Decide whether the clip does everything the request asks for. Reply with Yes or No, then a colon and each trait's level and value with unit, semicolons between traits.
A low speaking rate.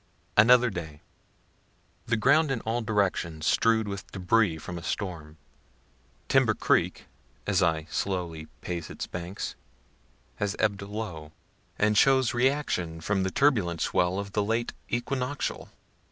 Yes: slow, 130 wpm